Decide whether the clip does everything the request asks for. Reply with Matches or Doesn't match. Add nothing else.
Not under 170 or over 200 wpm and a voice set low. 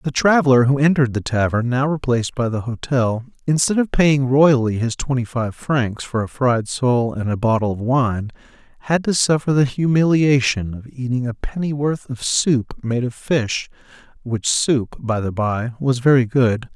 Matches